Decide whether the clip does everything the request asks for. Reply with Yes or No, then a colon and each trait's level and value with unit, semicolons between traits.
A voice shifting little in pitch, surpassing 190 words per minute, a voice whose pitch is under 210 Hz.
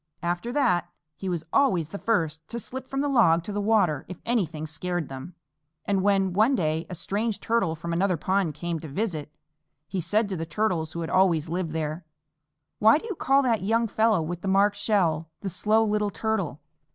No: average, 4.9 semitones; average, 200 wpm; medium, 185 Hz